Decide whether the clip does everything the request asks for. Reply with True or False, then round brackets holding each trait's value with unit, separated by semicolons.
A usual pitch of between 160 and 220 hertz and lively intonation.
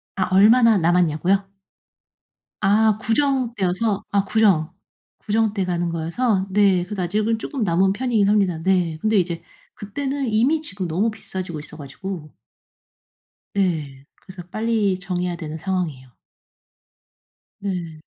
False (190 Hz; 3.8 semitones)